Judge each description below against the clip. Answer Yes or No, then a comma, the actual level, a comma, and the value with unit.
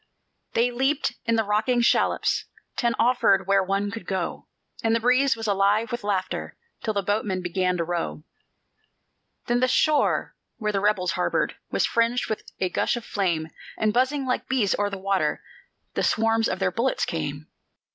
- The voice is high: Yes, high, 215 Hz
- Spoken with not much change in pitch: No, average, 3.7 semitones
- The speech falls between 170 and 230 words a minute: Yes, average, 175 wpm